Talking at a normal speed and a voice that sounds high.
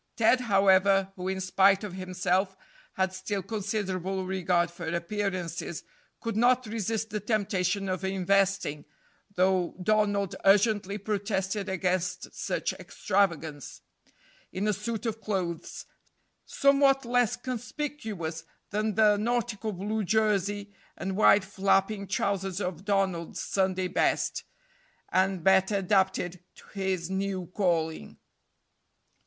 No: slow, 115 wpm; high, 195 Hz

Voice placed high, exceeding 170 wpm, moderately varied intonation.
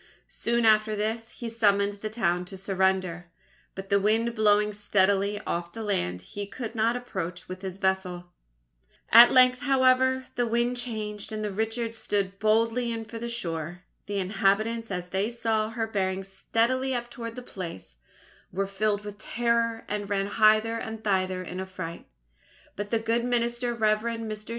No: high, 215 Hz; average, 165 wpm; average, 3.1 semitones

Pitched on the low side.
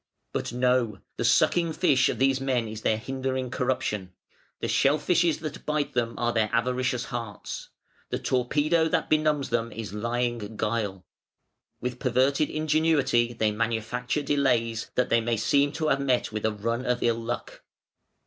Yes: low, 125 Hz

